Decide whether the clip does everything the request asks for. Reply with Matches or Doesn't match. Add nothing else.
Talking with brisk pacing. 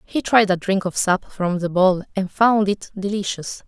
Matches